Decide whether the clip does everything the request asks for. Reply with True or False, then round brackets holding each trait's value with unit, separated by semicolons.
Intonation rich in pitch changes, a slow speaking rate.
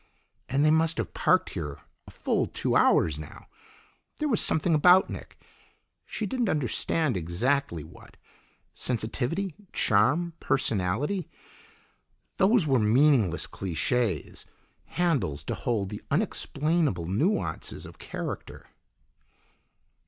True (8.8 semitones; 110 wpm)